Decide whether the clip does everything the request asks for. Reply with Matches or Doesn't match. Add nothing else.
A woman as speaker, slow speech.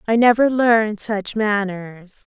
Matches